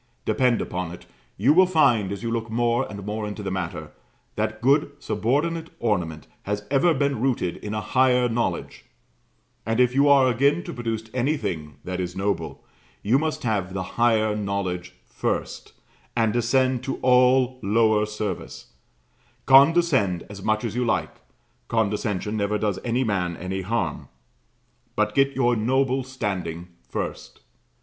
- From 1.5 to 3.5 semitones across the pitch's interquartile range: No, average, 4.6 semitones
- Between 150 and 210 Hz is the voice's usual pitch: No, low, 110 Hz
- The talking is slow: No, average, 150 wpm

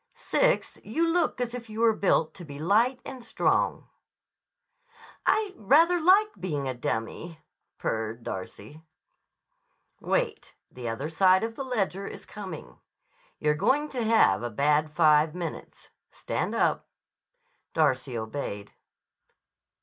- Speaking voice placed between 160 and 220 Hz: Yes, medium, 185 Hz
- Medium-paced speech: No, slow, 125 wpm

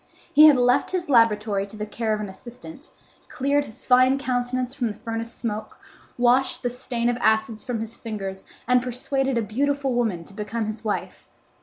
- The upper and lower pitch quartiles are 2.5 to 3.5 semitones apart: Yes, average, 2.9 semitones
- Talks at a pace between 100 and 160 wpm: No, average, 185 wpm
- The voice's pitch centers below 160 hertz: No, high, 240 Hz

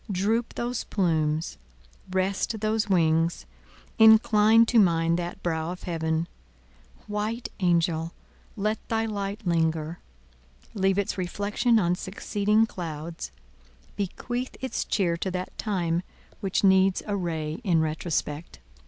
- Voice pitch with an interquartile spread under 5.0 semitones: Yes, average, 4.2 semitones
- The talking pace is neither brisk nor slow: No, slow, 120 wpm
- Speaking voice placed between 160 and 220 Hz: Yes, medium, 185 Hz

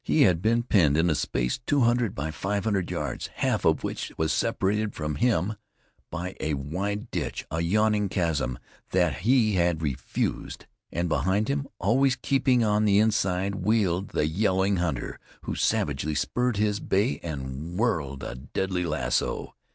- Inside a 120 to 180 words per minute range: Yes, average, 160 wpm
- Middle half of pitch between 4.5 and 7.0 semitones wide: Yes, average, 5.2 semitones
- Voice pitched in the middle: No, very low, 95 Hz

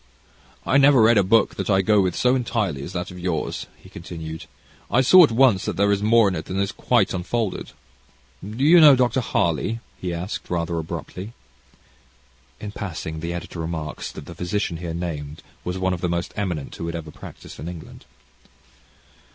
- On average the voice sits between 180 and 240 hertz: No, very low, 95 Hz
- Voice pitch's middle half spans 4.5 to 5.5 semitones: Yes, average, 4.8 semitones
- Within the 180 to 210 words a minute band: Yes, average, 190 wpm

